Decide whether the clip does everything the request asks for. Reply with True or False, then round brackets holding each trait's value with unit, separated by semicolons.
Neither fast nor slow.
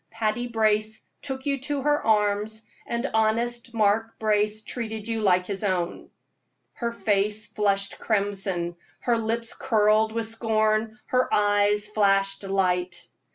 False (130 wpm)